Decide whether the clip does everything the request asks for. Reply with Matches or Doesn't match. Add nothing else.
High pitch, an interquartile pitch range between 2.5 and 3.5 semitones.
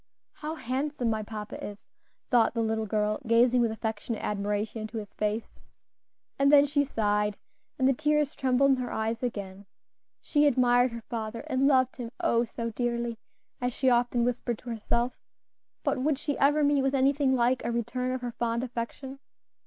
Matches